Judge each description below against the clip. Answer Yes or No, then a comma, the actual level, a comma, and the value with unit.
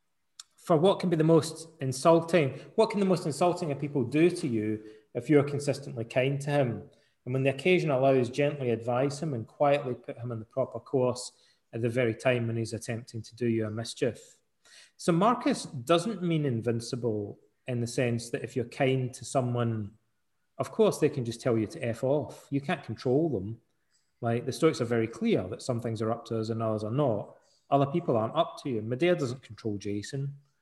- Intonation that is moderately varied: Yes, average, 4.3 semitones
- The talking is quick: Yes, fast, 210 wpm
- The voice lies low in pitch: Yes, low, 130 Hz